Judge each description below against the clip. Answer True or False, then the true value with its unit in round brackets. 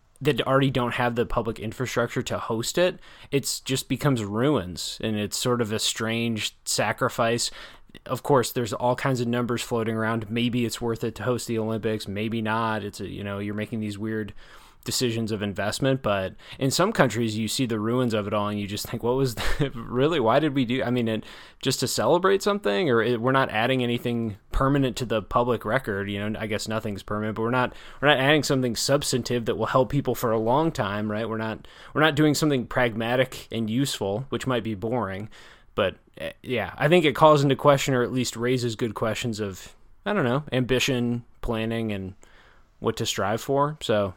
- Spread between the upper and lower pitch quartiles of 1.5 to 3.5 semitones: True (3.1 semitones)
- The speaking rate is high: True (210 wpm)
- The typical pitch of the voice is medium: False (120 Hz)